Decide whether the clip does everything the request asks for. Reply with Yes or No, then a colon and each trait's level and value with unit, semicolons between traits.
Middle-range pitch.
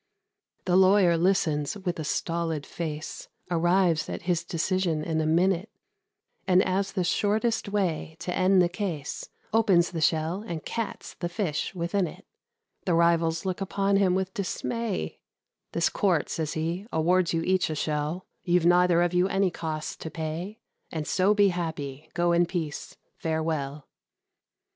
Yes: medium, 175 Hz